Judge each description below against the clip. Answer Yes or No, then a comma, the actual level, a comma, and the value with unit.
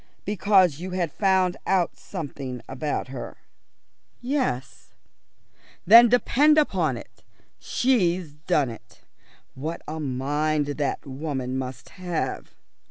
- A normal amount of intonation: No, wide, 5.7 semitones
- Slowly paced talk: Yes, slow, 105 wpm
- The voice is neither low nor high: Yes, medium, 160 Hz